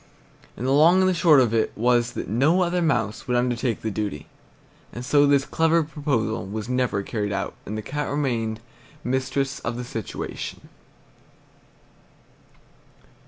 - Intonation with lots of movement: No, average, 4.6 semitones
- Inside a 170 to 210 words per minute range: No, average, 155 wpm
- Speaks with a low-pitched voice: Yes, low, 125 Hz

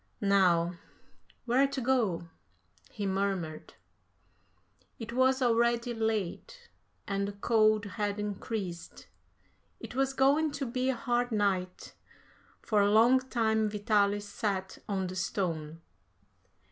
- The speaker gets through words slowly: Yes, slow, 115 wpm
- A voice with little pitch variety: No, average, 3.9 semitones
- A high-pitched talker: Yes, high, 215 Hz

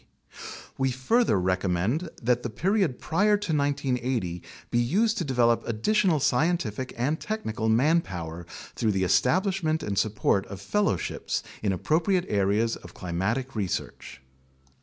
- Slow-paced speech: Yes, slow, 125 wpm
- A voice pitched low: Yes, low, 125 Hz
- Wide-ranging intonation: Yes, wide, 8.4 semitones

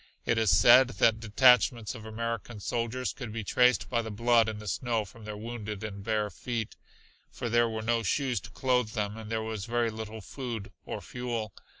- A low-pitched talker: Yes, low, 115 Hz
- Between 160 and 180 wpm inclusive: No, fast, 205 wpm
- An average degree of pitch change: No, narrow, 2.0 semitones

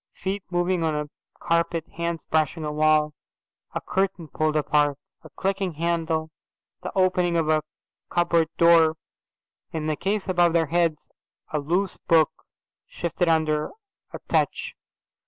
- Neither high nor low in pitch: Yes, medium, 165 Hz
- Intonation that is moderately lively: No, narrow, 2.2 semitones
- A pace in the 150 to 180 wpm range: No, slow, 135 wpm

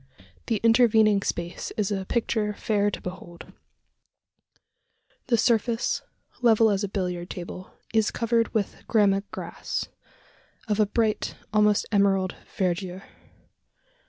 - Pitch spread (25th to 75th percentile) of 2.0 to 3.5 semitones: Yes, average, 2.8 semitones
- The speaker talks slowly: Yes, slow, 115 wpm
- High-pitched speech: Yes, high, 210 Hz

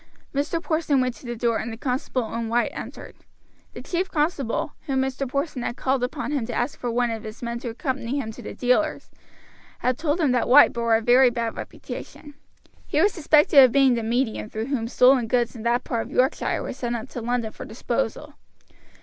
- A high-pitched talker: Yes, very high, 250 Hz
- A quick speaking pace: Yes, fast, 215 wpm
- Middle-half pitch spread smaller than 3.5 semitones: Yes, average, 3.0 semitones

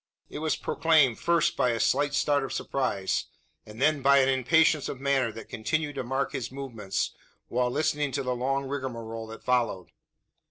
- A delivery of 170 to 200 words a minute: Yes, average, 175 wpm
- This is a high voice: No, low, 135 Hz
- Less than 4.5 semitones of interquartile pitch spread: Yes, average, 3.4 semitones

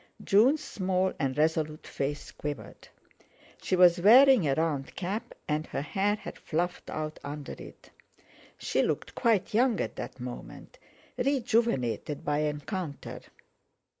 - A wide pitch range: Yes, wide, 6.2 semitones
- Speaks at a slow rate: Yes, slow, 130 wpm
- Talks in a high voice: No, medium, 170 Hz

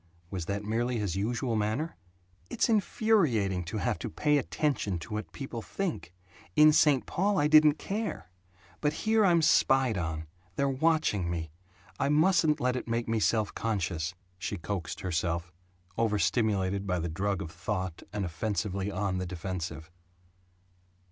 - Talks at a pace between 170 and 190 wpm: No, average, 150 wpm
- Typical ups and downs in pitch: No, wide, 7.9 semitones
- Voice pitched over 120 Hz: No, low, 105 Hz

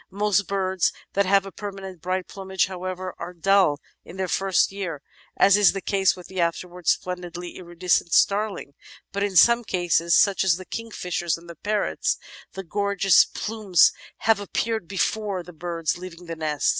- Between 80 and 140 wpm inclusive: No, average, 170 wpm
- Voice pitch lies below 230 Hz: Yes, medium, 185 Hz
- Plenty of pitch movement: No, narrow, 2.4 semitones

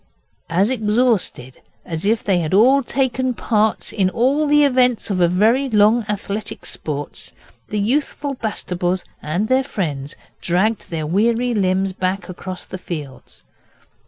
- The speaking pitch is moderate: No, high, 210 Hz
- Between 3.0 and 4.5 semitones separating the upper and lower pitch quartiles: No, average, 5.2 semitones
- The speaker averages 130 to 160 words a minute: Yes, average, 140 wpm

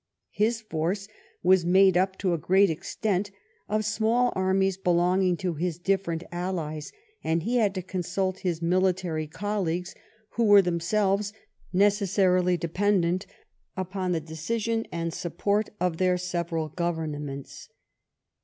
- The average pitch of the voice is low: No, medium, 185 Hz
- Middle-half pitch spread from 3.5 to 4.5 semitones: No, average, 2.7 semitones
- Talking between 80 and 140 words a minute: Yes, slow, 135 wpm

